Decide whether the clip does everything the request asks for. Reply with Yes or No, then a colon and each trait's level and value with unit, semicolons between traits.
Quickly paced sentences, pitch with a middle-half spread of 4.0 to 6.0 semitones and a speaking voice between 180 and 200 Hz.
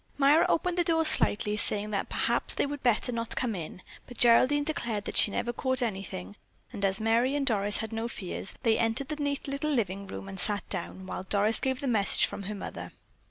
No: fast, 215 wpm; average, 5.2 semitones; high, 225 Hz